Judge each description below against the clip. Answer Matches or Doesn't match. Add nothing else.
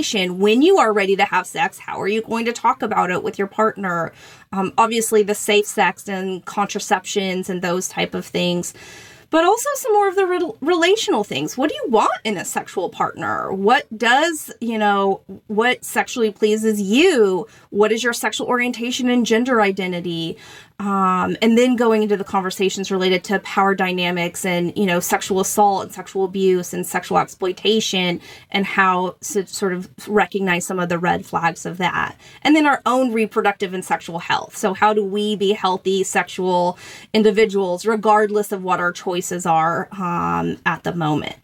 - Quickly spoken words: Doesn't match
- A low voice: Doesn't match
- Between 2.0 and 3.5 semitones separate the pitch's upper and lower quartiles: Matches